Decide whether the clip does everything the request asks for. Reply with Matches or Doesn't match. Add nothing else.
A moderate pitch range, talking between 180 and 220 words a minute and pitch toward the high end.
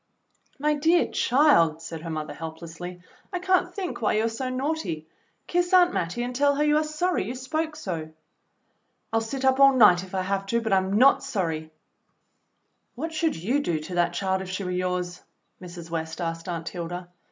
Doesn't match